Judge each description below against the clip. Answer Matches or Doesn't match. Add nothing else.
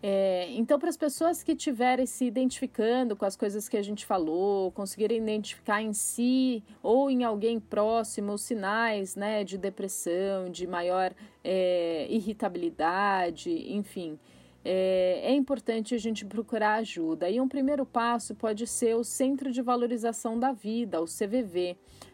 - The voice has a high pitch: Matches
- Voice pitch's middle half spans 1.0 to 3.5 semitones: Doesn't match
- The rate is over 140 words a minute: Matches